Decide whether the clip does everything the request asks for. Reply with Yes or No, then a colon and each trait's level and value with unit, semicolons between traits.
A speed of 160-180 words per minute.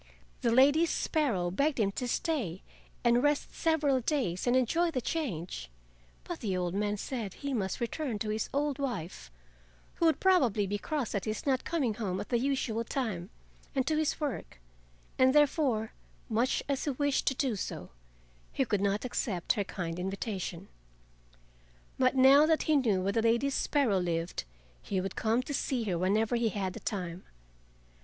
Yes: average, 175 wpm